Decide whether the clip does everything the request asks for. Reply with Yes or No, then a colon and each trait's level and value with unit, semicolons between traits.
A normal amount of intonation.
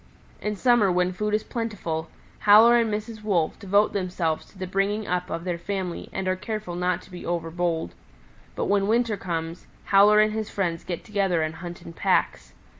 Yes: average, 3.4 semitones